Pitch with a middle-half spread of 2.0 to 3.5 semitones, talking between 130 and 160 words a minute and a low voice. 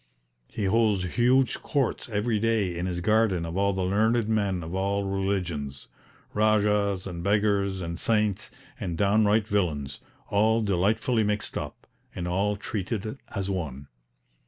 Yes: average, 2.9 semitones; average, 140 wpm; low, 100 Hz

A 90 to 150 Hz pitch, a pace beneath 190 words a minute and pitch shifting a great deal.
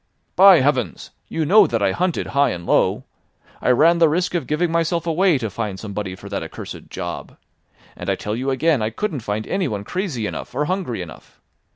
No: medium, 140 Hz; average, 200 wpm; wide, 8.0 semitones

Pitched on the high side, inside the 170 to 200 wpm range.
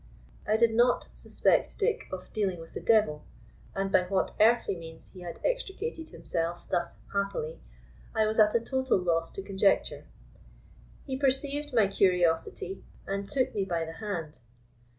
No: high, 200 Hz; average, 155 wpm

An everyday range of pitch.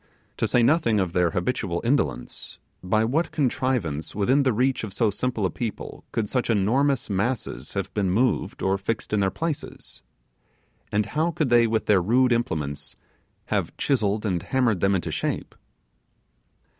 Yes: average, 4.8 semitones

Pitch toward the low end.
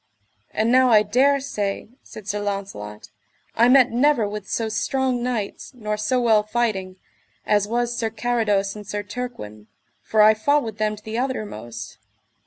No: high, 215 Hz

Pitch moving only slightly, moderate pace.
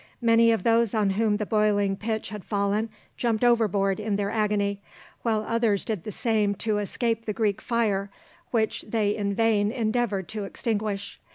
Yes: narrow, 2.0 semitones; average, 170 wpm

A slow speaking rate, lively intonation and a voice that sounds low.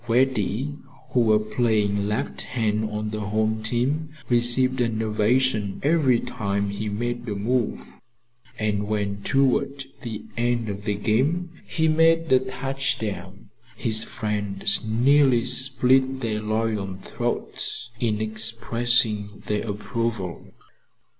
No: slow, 120 wpm; average, 3.5 semitones; low, 115 Hz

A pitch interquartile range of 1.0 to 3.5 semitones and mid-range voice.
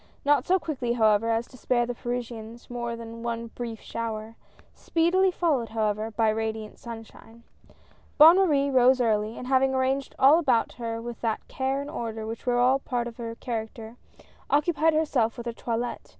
No: average, 2.8 semitones; high, 240 Hz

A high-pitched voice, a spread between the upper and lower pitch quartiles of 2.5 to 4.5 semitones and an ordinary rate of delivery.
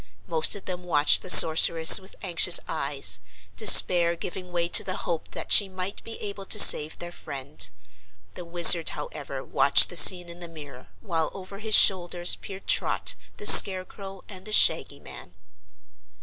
No: medium, 175 Hz; average, 2.8 semitones; average, 165 wpm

